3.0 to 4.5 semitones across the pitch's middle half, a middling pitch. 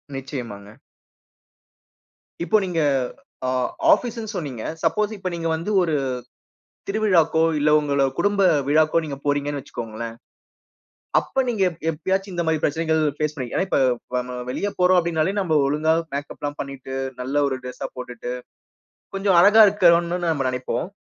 No: average, 5.1 semitones; medium, 160 Hz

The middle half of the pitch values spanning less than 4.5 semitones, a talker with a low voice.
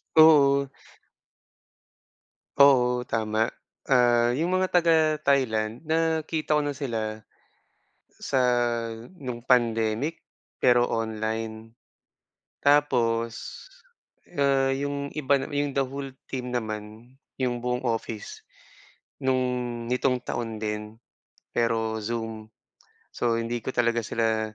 Yes: average, 3.6 semitones; low, 120 Hz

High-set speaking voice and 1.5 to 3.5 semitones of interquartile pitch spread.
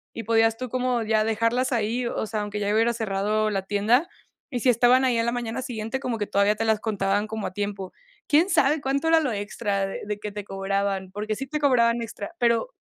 Yes: high, 225 Hz; average, 3.0 semitones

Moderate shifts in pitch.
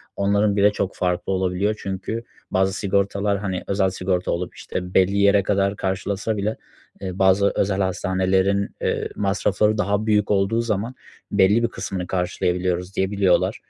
No: narrow, 1.5 semitones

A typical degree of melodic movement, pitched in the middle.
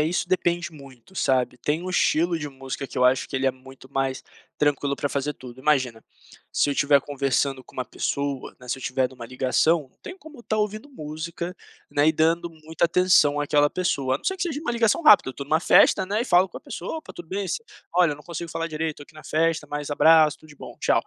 Yes: average, 4.3 semitones; medium, 150 Hz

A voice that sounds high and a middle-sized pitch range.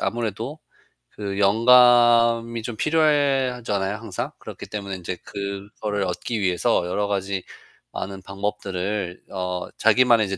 No: low, 105 Hz; average, 3.3 semitones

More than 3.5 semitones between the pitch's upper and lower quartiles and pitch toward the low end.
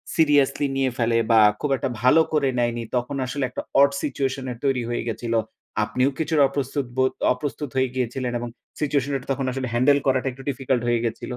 No: narrow, 2.5 semitones; low, 130 Hz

